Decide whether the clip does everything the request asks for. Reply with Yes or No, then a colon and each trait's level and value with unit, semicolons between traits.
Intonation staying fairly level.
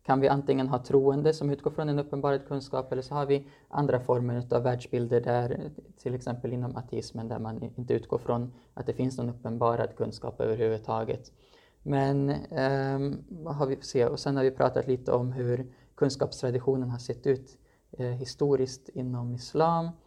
Yes: narrow, 2.3 semitones